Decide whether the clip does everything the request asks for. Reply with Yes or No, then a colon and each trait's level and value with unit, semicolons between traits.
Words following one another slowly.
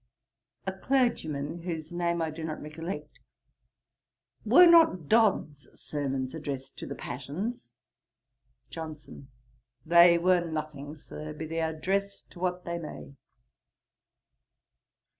Yes: slow, 110 wpm